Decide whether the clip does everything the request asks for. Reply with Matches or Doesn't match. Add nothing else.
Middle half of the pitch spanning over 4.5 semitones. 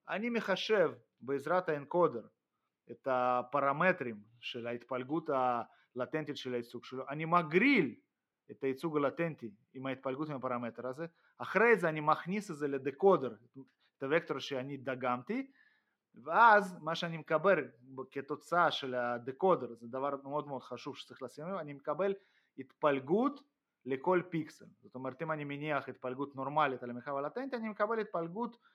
Matches